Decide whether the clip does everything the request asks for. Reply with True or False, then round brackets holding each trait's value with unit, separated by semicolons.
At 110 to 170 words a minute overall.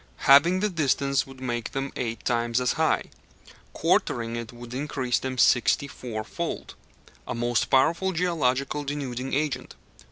True (140 wpm)